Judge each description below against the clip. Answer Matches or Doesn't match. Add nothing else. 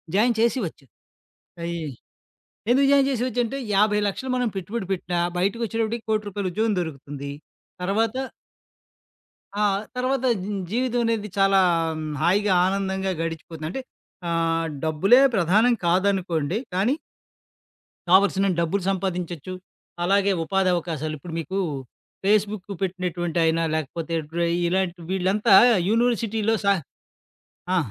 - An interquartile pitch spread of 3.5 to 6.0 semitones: Matches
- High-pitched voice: Matches